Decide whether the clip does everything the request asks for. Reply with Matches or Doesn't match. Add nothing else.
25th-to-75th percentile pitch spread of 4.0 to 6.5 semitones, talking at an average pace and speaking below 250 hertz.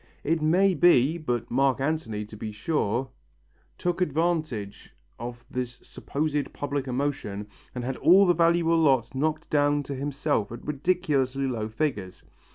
Matches